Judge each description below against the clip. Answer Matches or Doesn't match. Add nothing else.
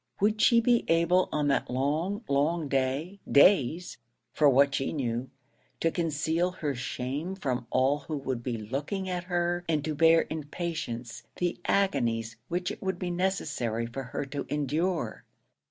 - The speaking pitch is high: Doesn't match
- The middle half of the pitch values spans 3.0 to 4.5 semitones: Doesn't match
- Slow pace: Doesn't match